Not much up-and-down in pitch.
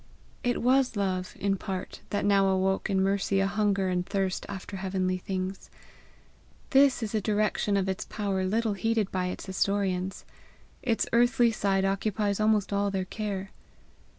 Yes: narrow, 1.9 semitones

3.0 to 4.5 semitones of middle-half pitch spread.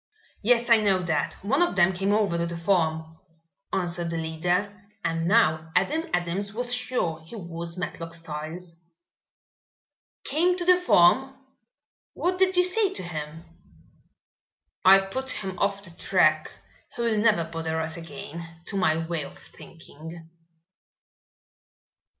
No: average, 5.0 semitones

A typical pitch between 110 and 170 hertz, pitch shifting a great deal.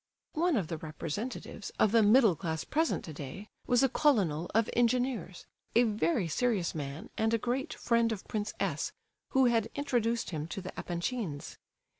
No: high, 215 Hz; wide, 6.3 semitones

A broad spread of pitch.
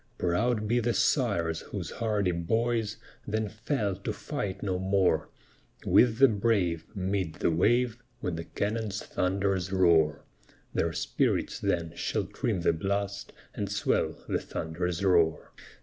No: average, 4.1 semitones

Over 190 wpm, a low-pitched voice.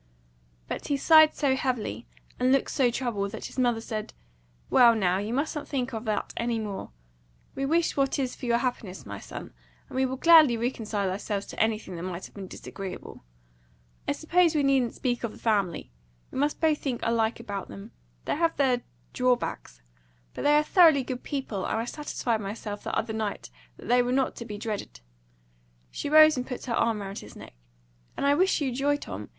No: average, 200 wpm; high, 240 Hz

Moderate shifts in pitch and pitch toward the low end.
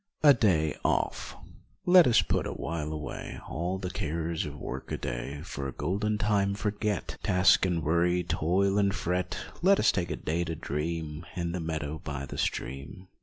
Yes: average, 4.3 semitones; very low, 85 Hz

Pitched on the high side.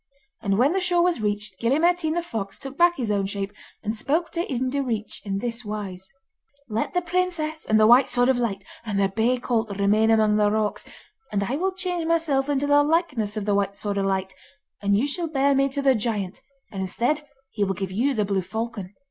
Yes: high, 230 Hz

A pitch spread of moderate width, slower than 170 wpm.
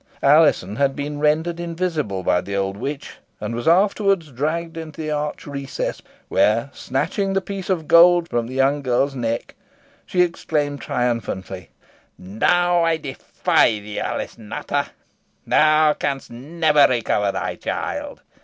No: wide, 5.7 semitones; average, 145 wpm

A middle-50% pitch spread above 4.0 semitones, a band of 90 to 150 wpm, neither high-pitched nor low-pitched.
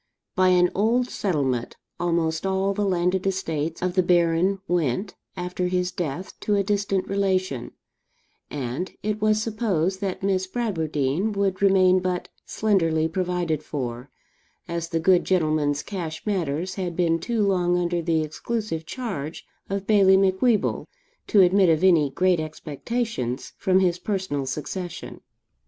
No: average, 3.3 semitones; average, 140 wpm; medium, 180 Hz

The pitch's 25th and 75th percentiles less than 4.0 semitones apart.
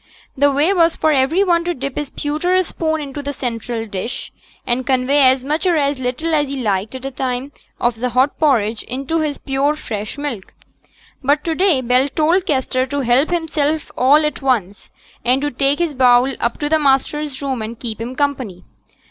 Yes: average, 3.3 semitones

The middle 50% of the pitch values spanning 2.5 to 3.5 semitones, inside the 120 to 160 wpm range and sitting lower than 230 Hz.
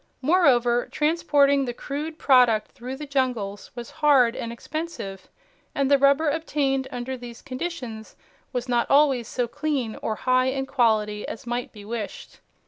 No: average, 3.1 semitones; average, 150 wpm; very high, 255 Hz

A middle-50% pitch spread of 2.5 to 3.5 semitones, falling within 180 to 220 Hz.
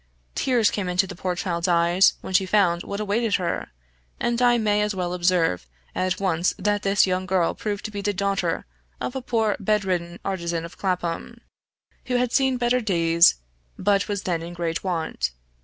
Yes: average, 3.2 semitones; high, 190 Hz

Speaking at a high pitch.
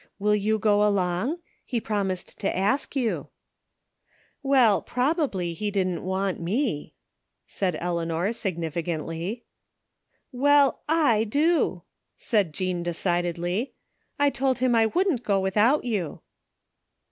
Yes: high, 205 Hz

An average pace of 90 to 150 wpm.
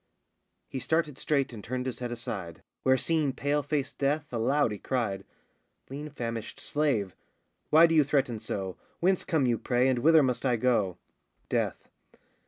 No: average, 165 wpm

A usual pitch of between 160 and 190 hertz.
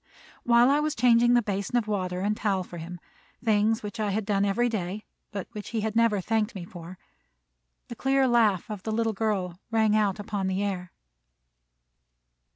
No: high, 210 Hz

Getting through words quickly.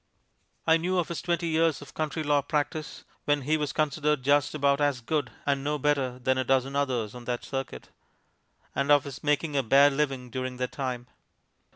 No: average, 195 wpm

